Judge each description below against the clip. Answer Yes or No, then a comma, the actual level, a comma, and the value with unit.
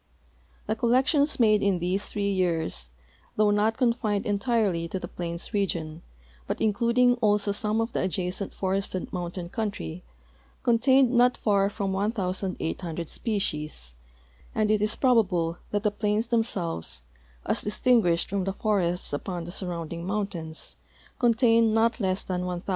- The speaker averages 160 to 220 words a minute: No, average, 140 wpm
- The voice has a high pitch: Yes, high, 200 Hz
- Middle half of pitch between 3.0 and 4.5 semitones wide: Yes, average, 4.0 semitones